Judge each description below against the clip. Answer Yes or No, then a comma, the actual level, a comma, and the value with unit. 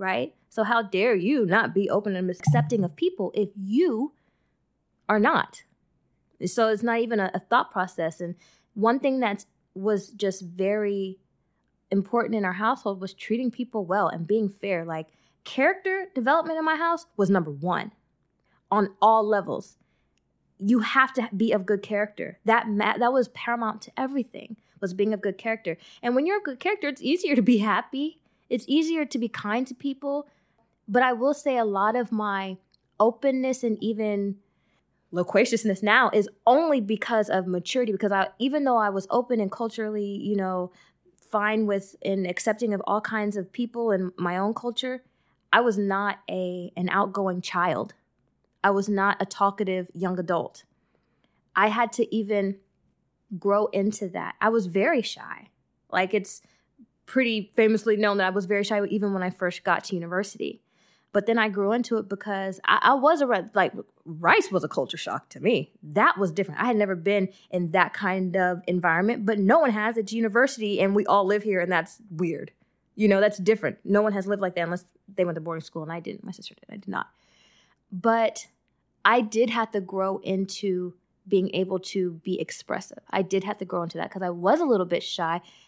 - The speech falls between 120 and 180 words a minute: No, average, 190 wpm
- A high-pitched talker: Yes, high, 205 Hz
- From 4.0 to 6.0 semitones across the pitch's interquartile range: No, average, 3.4 semitones